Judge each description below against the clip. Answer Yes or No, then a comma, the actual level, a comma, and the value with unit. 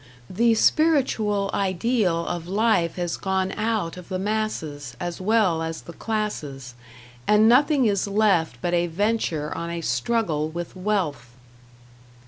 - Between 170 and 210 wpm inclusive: No, slow, 135 wpm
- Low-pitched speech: No, high, 190 Hz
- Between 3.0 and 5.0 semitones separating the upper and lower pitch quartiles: Yes, average, 4.5 semitones